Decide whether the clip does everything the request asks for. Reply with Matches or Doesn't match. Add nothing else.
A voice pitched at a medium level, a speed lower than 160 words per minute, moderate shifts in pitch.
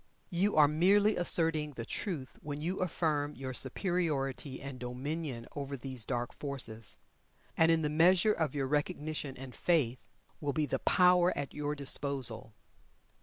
Matches